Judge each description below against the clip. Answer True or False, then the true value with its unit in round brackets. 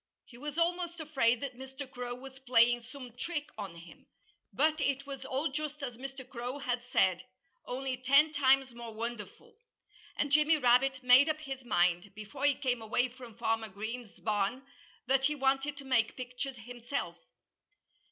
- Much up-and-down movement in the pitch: False (2.8 semitones)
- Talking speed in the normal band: True (165 wpm)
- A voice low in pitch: False (255 Hz)